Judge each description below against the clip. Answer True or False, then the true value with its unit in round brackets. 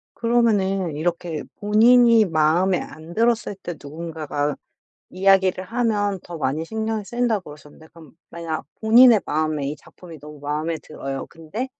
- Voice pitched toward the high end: False (175 Hz)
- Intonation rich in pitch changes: True (5.8 semitones)